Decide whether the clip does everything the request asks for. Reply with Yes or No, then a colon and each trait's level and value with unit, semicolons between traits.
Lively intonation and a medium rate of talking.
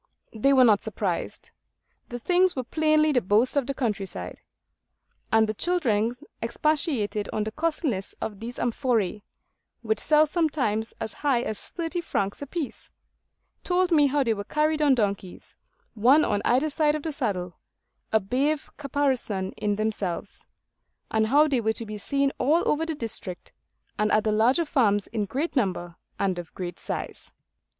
Yes: wide, 5.9 semitones; average, 160 wpm